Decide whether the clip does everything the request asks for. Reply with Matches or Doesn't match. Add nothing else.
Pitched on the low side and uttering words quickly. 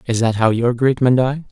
Matches